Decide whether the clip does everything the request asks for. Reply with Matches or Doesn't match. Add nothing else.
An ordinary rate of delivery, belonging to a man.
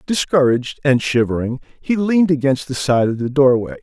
Matches